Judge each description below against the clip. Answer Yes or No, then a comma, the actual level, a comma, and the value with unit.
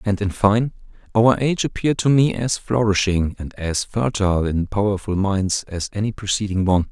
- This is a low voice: Yes, low, 105 Hz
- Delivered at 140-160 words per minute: No, average, 175 wpm